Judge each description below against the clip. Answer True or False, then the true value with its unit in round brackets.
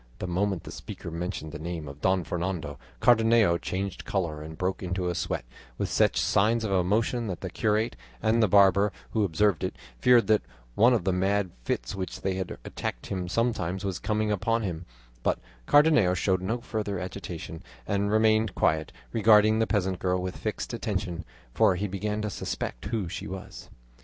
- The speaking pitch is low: True (95 Hz)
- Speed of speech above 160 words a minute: True (180 wpm)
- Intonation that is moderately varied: True (3.3 semitones)